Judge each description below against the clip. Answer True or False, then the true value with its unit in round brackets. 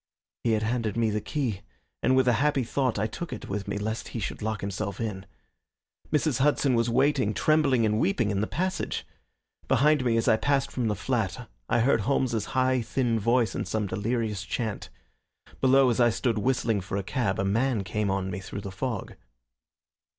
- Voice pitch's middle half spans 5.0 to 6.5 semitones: False (3.8 semitones)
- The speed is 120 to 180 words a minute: False (195 wpm)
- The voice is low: True (115 Hz)